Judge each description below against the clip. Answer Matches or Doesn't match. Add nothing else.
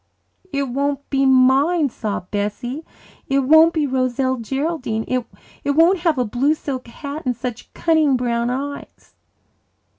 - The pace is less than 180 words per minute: Matches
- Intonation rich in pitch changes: Doesn't match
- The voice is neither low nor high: Doesn't match